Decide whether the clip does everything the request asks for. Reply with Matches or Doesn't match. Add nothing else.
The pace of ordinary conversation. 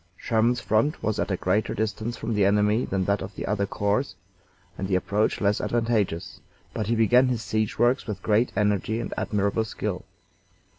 Matches